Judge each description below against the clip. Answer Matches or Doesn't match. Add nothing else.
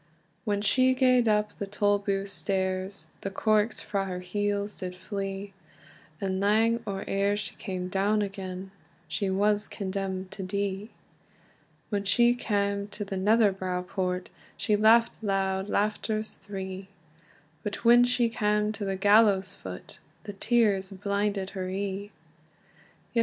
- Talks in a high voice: Matches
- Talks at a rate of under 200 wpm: Matches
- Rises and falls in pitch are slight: Matches